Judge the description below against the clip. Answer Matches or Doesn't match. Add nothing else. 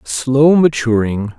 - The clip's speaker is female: Doesn't match